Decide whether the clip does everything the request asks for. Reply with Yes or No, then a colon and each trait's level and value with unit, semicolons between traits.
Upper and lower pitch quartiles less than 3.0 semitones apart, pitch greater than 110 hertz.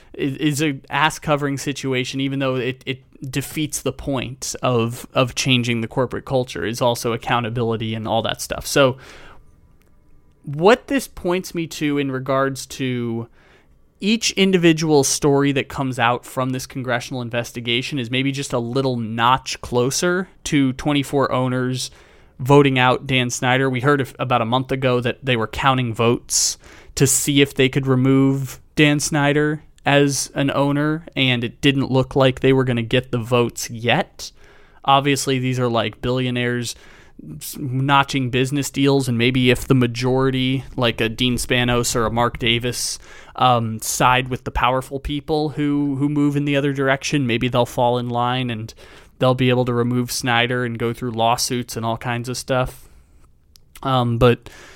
Yes: narrow, 2.5 semitones; low, 130 Hz